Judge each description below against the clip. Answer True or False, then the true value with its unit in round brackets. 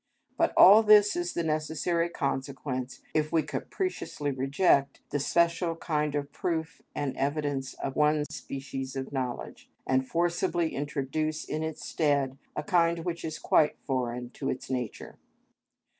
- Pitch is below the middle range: False (150 Hz)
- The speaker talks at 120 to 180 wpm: True (145 wpm)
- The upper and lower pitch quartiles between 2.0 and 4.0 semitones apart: True (3.7 semitones)